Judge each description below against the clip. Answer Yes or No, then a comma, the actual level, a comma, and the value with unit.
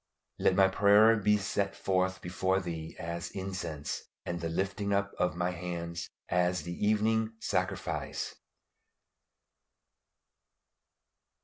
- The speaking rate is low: Yes, slow, 110 wpm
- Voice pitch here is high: No, very low, 95 Hz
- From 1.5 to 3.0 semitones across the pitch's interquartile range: Yes, average, 2.7 semitones